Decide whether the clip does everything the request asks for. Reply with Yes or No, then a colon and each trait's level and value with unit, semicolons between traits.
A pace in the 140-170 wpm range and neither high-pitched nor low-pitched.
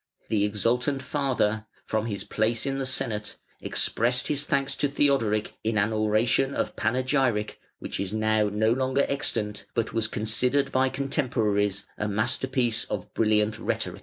No: average, 150 wpm; low, 115 Hz